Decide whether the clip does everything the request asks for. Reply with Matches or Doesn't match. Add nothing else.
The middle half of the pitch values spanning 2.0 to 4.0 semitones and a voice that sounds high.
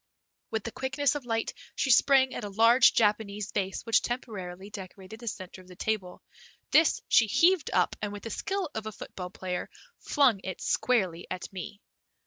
Doesn't match